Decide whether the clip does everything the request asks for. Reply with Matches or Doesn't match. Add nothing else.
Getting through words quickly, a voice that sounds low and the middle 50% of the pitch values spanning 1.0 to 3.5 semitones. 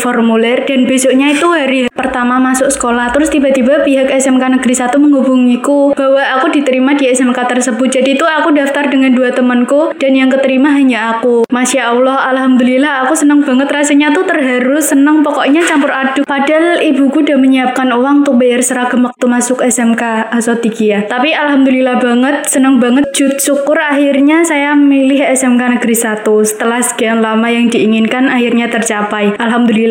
Doesn't match